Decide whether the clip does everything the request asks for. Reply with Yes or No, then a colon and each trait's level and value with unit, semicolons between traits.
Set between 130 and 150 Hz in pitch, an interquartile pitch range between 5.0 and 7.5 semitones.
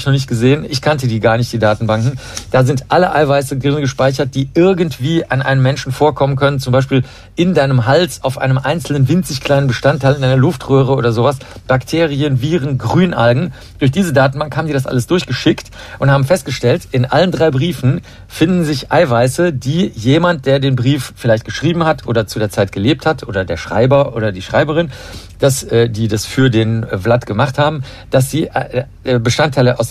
No: low, 135 Hz; average, 3.7 semitones